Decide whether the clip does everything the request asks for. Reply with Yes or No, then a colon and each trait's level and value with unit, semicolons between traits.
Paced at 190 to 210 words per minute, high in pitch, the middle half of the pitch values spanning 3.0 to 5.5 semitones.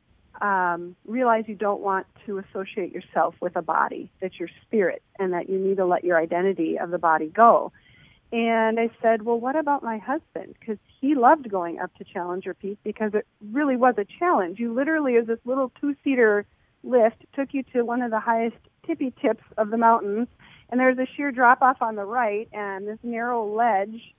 Yes: average, 200 wpm; high, 220 Hz; average, 4.0 semitones